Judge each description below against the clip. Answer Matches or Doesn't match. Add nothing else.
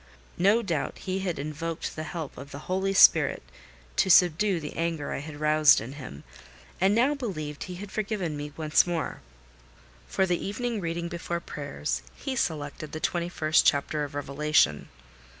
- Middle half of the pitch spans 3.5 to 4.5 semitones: Matches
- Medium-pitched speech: Matches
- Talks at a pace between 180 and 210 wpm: Doesn't match